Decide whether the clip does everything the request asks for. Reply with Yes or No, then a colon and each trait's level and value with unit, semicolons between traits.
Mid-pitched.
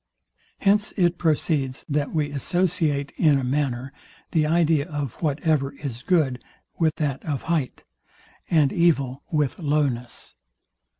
Yes: medium, 150 Hz